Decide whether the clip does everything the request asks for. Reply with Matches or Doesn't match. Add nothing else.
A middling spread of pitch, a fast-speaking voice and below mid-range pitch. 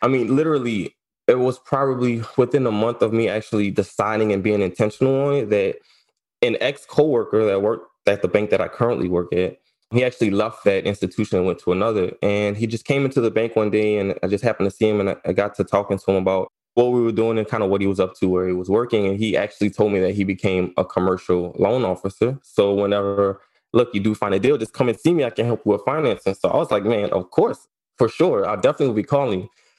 Matches